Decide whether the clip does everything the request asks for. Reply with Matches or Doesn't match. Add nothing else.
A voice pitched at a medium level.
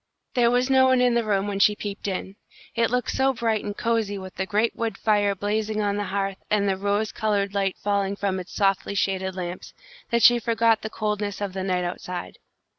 Doesn't match